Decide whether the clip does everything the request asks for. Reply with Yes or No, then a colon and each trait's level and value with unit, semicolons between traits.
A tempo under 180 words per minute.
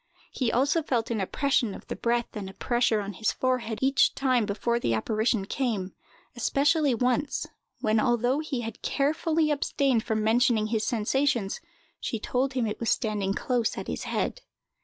Yes: average, 170 wpm